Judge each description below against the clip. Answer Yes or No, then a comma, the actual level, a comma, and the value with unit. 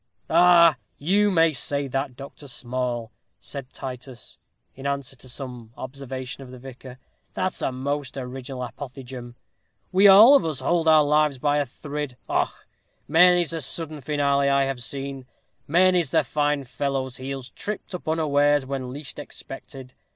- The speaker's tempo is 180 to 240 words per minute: No, average, 150 wpm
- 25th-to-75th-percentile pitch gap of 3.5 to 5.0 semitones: No, average, 3.0 semitones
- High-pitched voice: No, medium, 140 Hz